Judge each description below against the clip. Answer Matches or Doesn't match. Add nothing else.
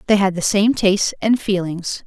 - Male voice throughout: Doesn't match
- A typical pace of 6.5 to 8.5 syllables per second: Doesn't match